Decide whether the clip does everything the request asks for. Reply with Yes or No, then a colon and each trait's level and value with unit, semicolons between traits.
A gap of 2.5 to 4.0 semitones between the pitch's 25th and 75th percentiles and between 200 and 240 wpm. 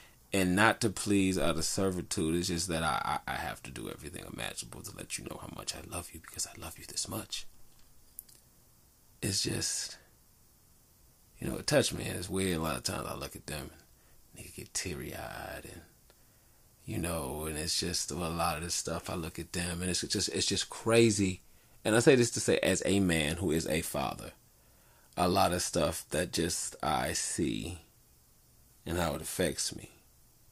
Yes: average, 3.2 semitones; fast, 205 wpm